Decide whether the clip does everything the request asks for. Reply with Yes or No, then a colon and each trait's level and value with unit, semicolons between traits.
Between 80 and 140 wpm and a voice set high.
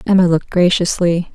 No: slow, 135 wpm; medium, 175 Hz